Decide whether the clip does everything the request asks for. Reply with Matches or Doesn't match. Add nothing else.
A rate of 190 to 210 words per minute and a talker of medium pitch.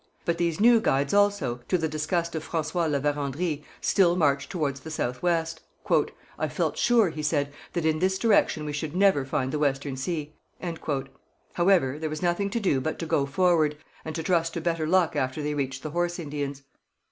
Matches